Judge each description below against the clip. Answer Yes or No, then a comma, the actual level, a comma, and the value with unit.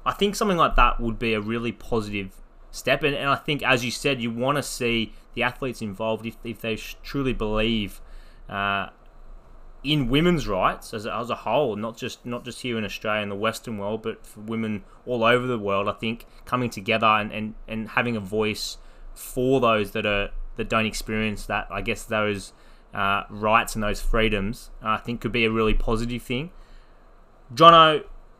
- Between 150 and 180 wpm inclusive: No, average, 190 wpm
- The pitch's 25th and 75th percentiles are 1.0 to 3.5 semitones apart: Yes, narrow, 2.5 semitones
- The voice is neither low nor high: No, low, 115 Hz